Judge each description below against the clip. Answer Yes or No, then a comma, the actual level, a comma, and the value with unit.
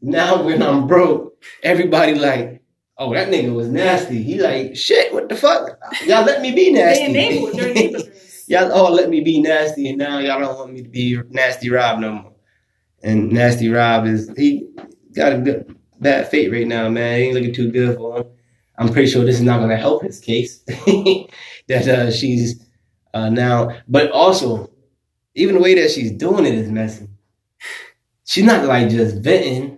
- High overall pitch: No, low, 125 Hz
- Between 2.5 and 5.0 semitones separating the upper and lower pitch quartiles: No, wide, 5.5 semitones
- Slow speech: No, average, 180 wpm